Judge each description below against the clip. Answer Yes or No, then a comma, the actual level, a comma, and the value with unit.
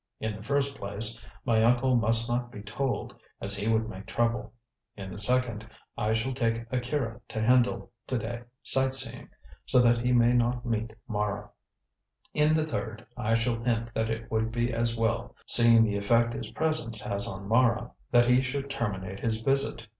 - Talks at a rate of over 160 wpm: Yes, average, 180 wpm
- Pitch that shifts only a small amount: Yes, narrow, 2.0 semitones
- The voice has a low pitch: Yes, low, 115 Hz